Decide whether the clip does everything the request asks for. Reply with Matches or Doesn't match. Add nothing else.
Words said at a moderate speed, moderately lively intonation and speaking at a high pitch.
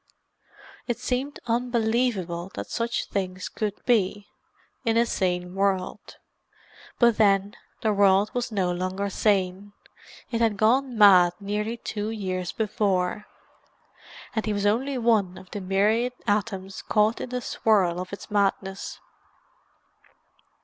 Doesn't match